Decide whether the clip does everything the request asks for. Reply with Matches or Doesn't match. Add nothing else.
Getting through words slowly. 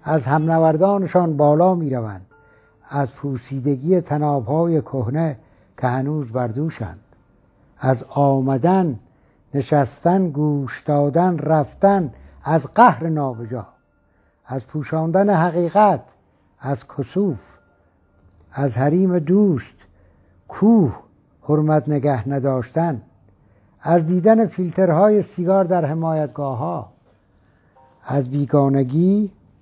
Matches